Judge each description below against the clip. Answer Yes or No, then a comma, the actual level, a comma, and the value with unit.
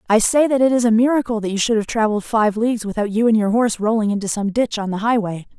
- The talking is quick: Yes, fast, 280 wpm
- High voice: Yes, high, 220 Hz